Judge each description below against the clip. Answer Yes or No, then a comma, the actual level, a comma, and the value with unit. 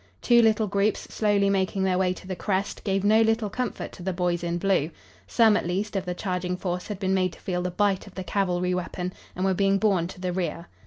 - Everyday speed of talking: No, fast, 245 wpm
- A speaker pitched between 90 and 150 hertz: No, high, 190 Hz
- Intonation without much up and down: Yes, narrow, 2.1 semitones